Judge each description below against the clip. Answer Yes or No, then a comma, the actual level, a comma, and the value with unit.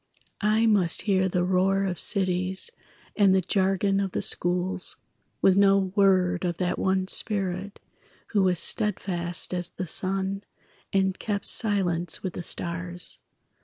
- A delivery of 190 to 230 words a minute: No, average, 140 wpm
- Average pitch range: No, narrow, 1.6 semitones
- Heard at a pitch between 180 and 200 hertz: Yes, high, 190 Hz